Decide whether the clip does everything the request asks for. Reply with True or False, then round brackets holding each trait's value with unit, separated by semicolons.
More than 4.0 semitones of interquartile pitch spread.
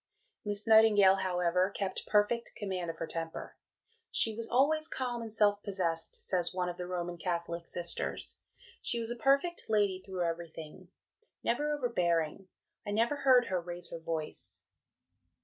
True (4.8 semitones)